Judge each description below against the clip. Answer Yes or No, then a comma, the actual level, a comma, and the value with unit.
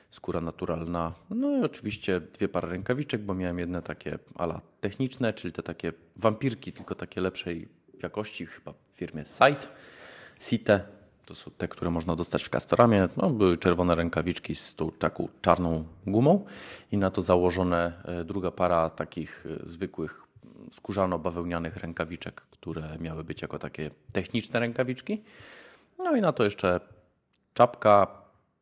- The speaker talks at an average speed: Yes, average, 140 wpm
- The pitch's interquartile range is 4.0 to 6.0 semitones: No, average, 3.6 semitones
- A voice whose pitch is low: Yes, very low, 90 Hz